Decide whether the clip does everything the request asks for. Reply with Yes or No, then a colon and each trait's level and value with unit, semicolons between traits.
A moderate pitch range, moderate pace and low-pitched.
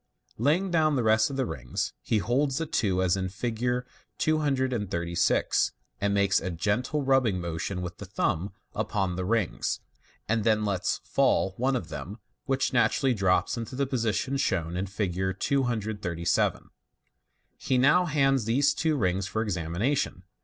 No: wide, 6.1 semitones; average, 155 wpm; low, 110 Hz